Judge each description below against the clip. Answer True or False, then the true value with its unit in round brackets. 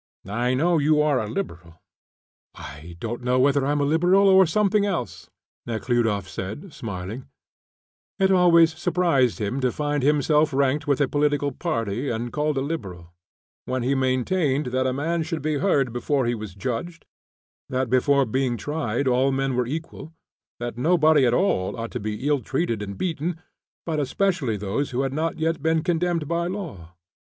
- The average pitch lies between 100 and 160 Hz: True (140 Hz)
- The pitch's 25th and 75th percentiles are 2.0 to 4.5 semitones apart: False (5.1 semitones)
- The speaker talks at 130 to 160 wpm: False (175 wpm)